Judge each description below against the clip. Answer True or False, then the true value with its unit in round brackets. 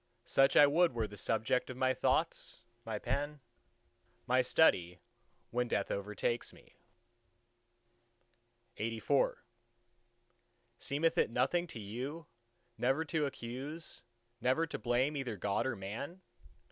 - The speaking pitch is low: True (130 Hz)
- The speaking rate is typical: False (120 wpm)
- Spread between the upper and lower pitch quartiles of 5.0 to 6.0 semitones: False (4.5 semitones)